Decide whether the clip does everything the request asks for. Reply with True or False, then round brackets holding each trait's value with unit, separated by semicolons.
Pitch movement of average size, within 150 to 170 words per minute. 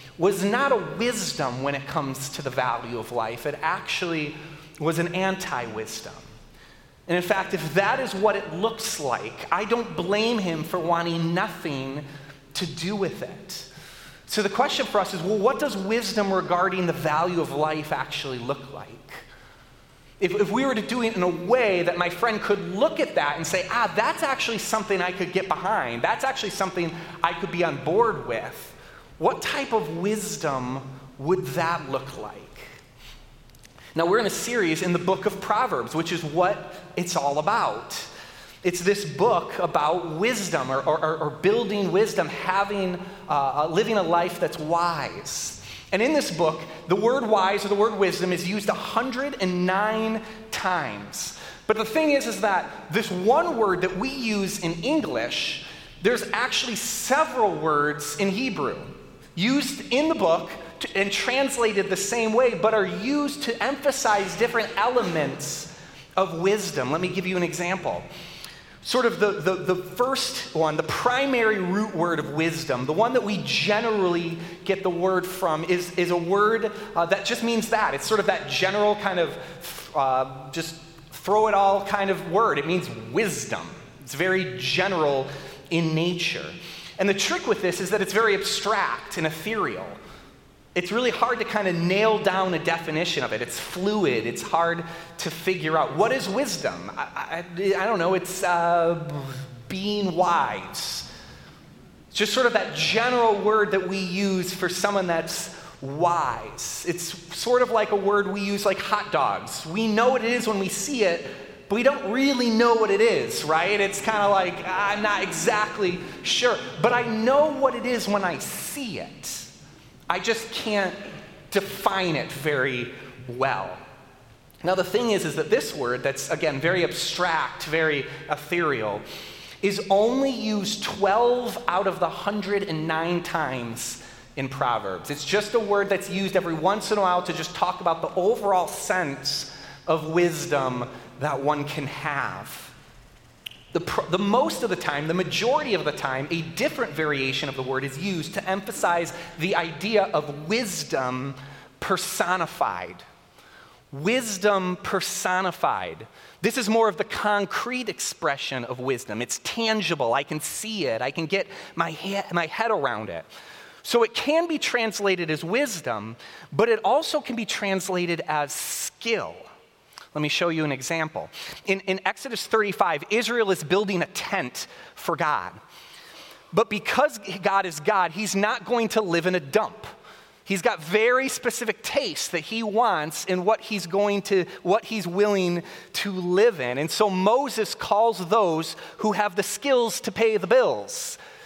True (4.7 semitones; 165 wpm)